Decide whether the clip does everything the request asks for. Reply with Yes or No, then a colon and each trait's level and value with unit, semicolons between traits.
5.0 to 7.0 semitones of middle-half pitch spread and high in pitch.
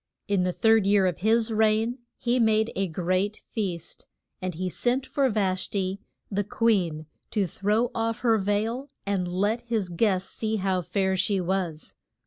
No: average, 3.2 semitones; high, 205 Hz